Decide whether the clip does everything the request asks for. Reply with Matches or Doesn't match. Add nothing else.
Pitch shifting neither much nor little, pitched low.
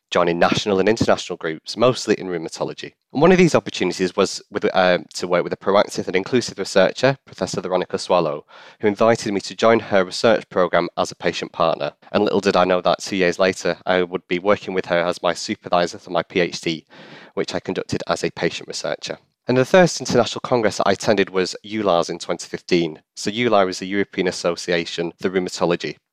Matches